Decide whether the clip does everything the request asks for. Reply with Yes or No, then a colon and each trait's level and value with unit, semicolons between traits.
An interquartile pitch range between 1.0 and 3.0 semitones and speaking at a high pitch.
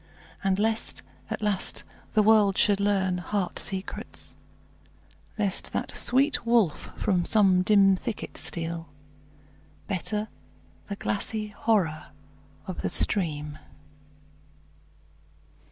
Yes: average, 2.7 semitones; high, 200 Hz